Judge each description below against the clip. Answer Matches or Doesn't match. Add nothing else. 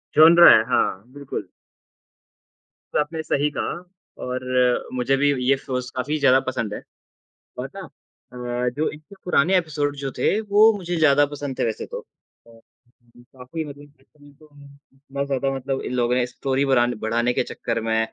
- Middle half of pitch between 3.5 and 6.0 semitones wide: Doesn't match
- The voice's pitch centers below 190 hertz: Matches